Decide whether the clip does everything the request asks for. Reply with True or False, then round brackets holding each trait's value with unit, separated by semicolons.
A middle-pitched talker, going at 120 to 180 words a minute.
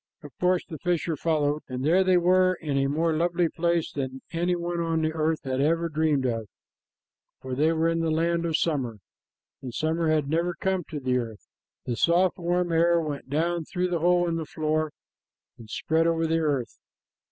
False (160 Hz; 200 wpm)